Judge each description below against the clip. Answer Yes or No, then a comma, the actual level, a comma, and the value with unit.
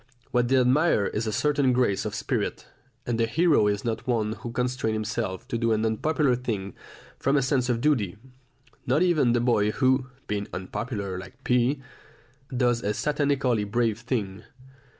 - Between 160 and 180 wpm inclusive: Yes, average, 170 wpm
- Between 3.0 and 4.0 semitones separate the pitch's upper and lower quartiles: Yes, average, 3.4 semitones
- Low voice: Yes, low, 120 Hz